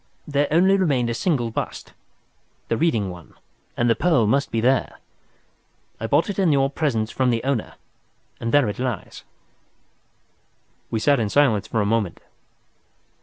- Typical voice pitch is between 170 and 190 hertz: No, low, 125 Hz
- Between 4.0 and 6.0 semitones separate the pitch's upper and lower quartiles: Yes, average, 4.5 semitones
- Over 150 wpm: No, average, 145 wpm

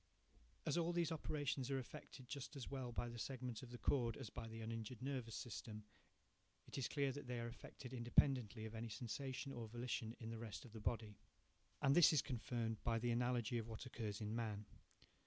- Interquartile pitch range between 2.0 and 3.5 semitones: Yes, average, 2.7 semitones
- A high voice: No, low, 120 Hz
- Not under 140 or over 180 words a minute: No, fast, 205 wpm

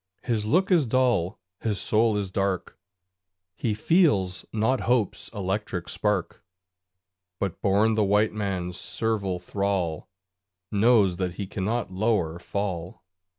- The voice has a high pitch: No, low, 105 Hz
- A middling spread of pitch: Yes, average, 3.1 semitones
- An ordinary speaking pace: No, slow, 120 wpm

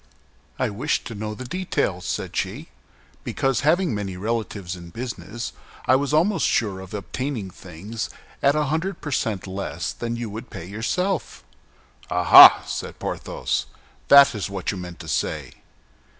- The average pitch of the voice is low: Yes, low, 110 Hz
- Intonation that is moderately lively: No, wide, 6.6 semitones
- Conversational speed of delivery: Yes, average, 160 wpm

